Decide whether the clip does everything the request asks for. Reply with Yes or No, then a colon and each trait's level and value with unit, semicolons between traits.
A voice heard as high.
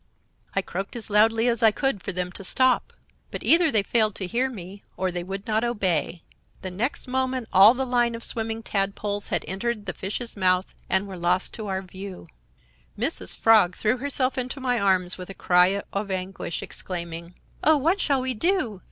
Yes: high, 205 Hz